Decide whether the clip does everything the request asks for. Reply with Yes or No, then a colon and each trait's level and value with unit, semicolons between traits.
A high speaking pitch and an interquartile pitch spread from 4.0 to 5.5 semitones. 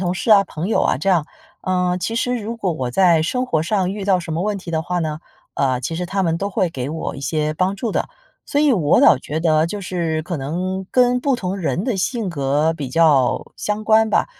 No: medium, 180 Hz; average, 4.3 semitones